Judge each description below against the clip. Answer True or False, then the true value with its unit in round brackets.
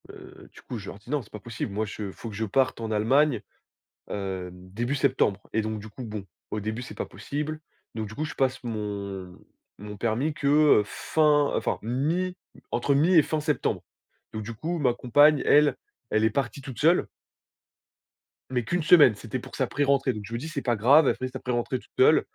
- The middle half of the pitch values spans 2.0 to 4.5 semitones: False (5.2 semitones)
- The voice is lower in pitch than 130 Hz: True (120 Hz)